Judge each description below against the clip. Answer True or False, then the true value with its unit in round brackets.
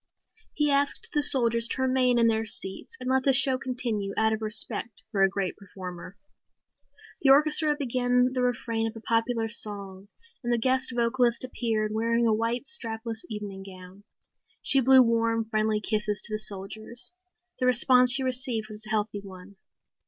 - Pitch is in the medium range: False (230 Hz)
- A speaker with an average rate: True (170 wpm)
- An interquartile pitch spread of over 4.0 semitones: False (3.0 semitones)